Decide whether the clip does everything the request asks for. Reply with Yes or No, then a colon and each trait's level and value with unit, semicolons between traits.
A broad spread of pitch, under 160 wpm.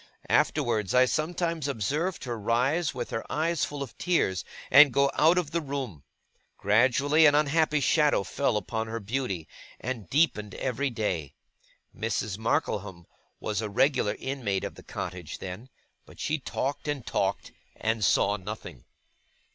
Yes: wide, 5.7 semitones; average, 145 wpm